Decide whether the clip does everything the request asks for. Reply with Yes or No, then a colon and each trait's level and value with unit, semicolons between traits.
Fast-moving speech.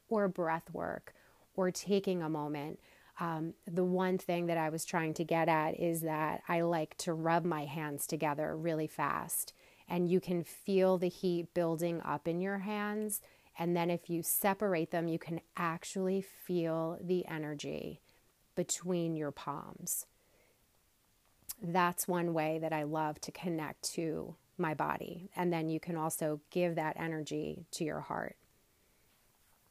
No: average, 155 wpm